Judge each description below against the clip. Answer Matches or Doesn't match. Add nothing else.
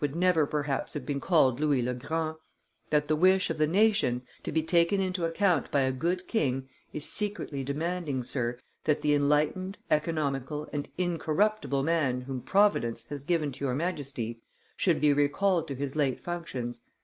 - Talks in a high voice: Doesn't match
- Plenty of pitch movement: Doesn't match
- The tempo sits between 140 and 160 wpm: Doesn't match